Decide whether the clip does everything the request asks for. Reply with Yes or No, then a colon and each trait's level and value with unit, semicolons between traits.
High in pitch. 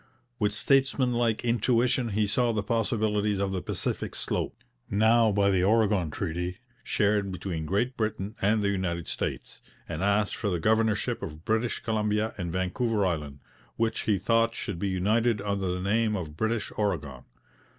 No: low, 105 Hz